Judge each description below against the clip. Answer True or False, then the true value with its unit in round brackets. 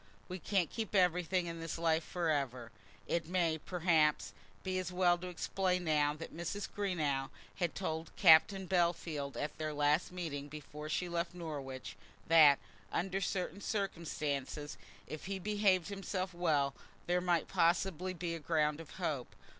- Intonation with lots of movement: False (3.2 semitones)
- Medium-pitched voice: True (170 Hz)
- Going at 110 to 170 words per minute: True (150 wpm)